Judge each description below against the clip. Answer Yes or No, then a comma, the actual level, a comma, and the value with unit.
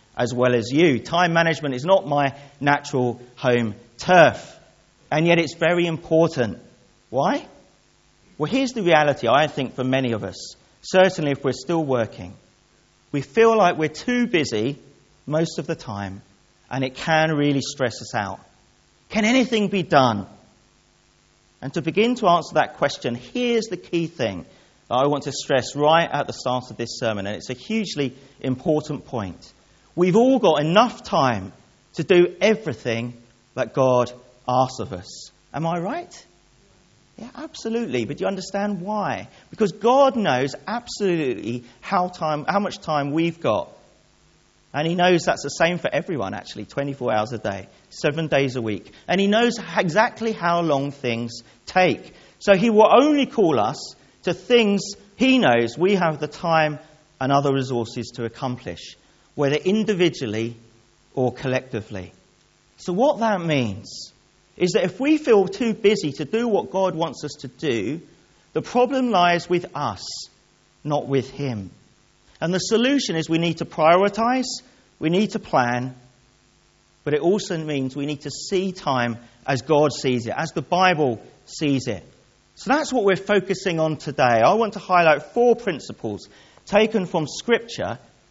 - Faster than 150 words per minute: Yes, average, 160 wpm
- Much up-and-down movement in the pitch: Yes, wide, 7.1 semitones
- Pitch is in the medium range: Yes, medium, 155 Hz